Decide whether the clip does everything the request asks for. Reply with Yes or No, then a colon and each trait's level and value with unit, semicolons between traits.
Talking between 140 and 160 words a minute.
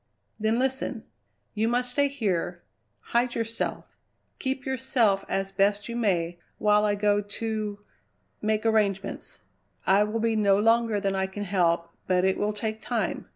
Yes: average, 155 wpm